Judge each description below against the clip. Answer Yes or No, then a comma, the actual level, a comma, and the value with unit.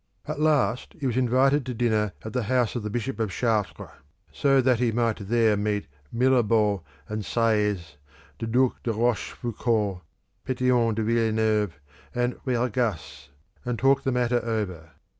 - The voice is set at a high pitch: No, low, 115 Hz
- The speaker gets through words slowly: No, average, 145 wpm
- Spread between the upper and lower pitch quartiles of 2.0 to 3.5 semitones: Yes, average, 2.7 semitones